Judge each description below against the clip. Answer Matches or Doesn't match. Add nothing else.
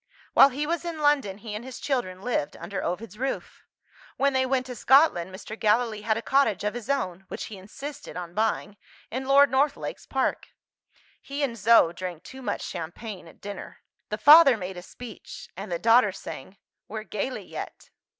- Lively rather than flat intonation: Matches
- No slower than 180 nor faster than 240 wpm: Matches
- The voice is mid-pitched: Doesn't match